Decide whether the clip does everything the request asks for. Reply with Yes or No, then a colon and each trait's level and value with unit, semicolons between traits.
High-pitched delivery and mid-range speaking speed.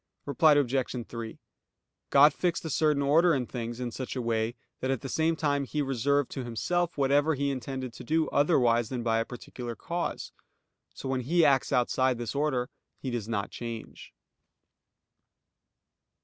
No: low, 135 Hz; average, 165 wpm